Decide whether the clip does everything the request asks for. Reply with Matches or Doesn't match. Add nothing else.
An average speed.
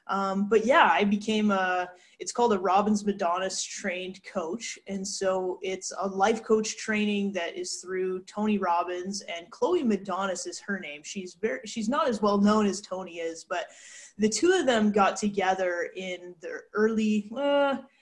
Matches